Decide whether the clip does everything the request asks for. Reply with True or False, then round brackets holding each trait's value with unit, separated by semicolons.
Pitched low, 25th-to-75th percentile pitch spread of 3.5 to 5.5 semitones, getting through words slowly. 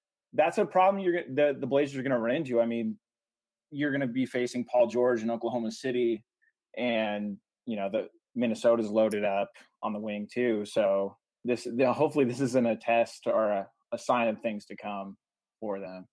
False (115 Hz; 3.9 semitones; 200 wpm)